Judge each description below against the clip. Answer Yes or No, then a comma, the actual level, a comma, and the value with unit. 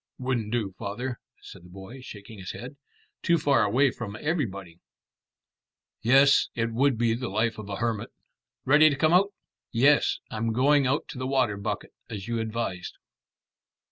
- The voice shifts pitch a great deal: No, average, 4.4 semitones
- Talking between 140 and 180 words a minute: Yes, average, 165 wpm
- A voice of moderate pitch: No, low, 120 Hz